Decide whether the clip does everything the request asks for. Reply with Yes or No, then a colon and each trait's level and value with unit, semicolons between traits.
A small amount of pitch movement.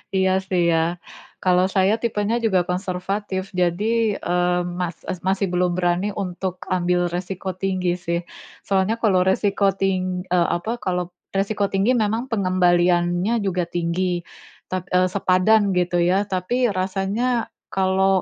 Yes: narrow, 1.5 semitones